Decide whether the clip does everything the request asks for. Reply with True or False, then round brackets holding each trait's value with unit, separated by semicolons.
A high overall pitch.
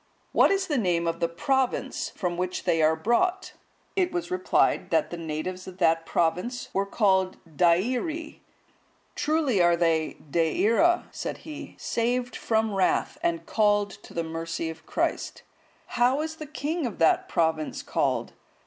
True (200 Hz)